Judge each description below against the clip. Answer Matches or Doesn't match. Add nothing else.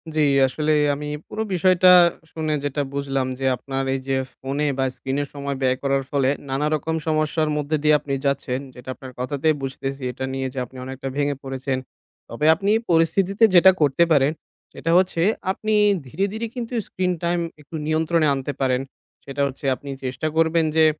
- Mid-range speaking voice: Matches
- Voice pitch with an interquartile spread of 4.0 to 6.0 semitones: Doesn't match